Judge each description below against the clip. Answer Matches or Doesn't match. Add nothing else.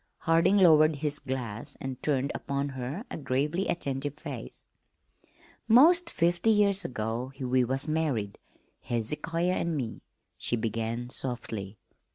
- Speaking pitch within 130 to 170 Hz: Matches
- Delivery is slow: Matches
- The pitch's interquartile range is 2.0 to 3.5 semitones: Doesn't match